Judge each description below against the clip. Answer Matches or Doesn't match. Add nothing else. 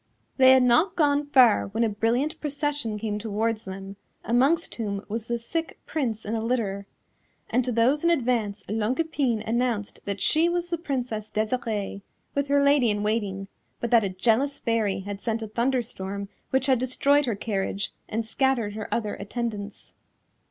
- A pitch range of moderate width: Matches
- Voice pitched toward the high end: Matches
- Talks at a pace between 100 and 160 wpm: Doesn't match